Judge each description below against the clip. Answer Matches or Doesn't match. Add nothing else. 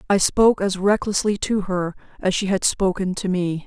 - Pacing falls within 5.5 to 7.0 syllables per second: Doesn't match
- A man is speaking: Doesn't match